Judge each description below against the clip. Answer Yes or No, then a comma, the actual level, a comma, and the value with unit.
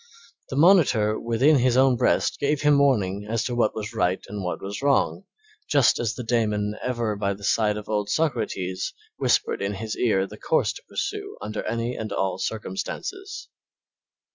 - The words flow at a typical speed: Yes, average, 175 wpm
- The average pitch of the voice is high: No, low, 110 Hz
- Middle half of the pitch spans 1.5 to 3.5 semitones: No, average, 4.3 semitones